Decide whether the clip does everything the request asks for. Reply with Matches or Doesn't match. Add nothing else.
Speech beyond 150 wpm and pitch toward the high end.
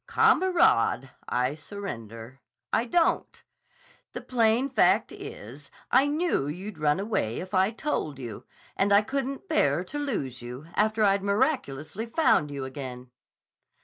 Doesn't match